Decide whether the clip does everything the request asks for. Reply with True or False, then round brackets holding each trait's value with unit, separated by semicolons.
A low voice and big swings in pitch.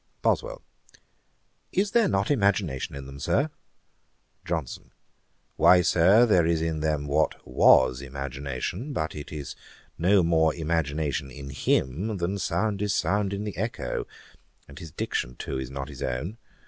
True (80 Hz; 6.4 semitones)